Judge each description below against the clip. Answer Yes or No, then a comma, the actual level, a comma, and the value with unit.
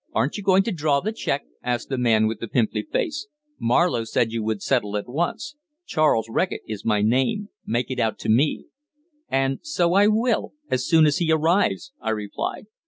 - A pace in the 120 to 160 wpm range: No, average, 195 wpm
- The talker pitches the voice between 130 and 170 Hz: Yes, low, 135 Hz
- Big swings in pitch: Yes, wide, 8.4 semitones